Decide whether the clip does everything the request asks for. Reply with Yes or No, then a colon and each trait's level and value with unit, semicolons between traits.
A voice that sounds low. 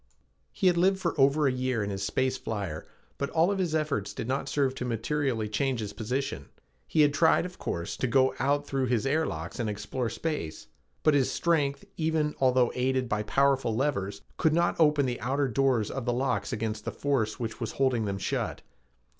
Yes: low, 130 Hz